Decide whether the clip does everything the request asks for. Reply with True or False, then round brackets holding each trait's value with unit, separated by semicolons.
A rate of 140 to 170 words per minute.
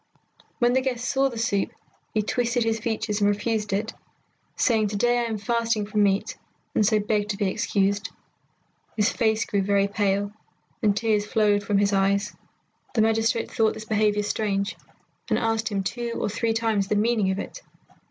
False (180 wpm)